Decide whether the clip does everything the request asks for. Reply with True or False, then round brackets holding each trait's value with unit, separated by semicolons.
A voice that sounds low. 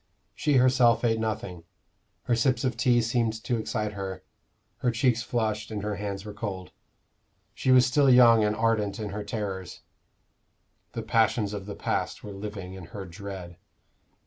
True (110 Hz)